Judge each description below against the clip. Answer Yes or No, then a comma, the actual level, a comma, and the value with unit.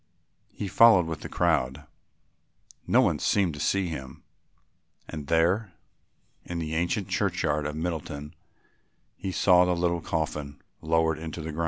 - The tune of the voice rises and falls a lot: No, average, 2.9 semitones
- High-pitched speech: No, very low, 80 Hz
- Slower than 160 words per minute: Yes, average, 145 wpm